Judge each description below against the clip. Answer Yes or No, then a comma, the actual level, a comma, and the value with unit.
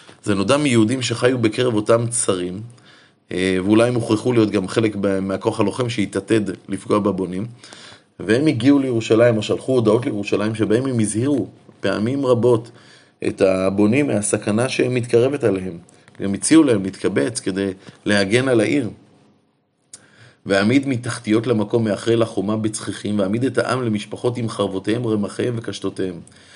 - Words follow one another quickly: No, average, 130 wpm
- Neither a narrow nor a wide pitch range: Yes, average, 3.3 semitones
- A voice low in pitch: Yes, low, 110 Hz